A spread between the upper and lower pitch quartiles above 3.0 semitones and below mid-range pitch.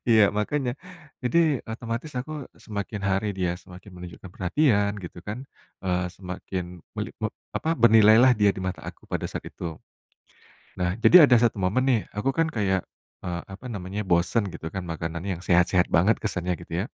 Yes: average, 4.2 semitones; low, 100 Hz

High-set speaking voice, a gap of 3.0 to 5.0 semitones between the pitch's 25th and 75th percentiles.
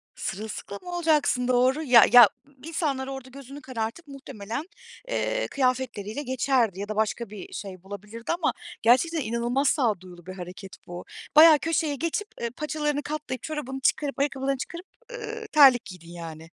No: very high, 260 Hz; wide, 5.6 semitones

